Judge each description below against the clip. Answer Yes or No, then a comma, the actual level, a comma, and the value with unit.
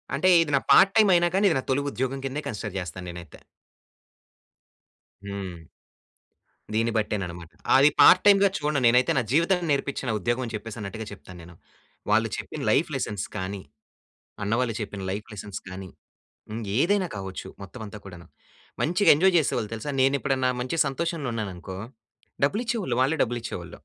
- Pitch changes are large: Yes, wide, 6.9 semitones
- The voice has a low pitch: Yes, low, 120 Hz